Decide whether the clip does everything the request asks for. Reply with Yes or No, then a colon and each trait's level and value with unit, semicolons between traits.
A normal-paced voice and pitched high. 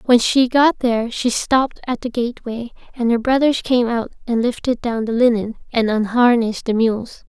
Yes: average, 190 wpm; high, 235 Hz